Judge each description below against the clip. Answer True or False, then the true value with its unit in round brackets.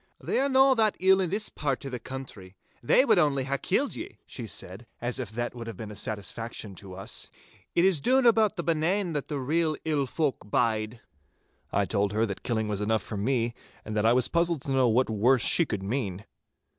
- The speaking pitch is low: True (125 Hz)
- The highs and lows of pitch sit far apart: True (7.4 semitones)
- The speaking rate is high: True (220 wpm)